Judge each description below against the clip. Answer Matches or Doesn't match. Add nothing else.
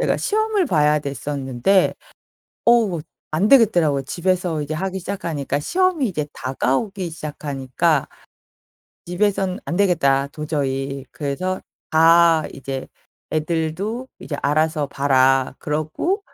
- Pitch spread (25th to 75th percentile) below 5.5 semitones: Matches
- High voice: Doesn't match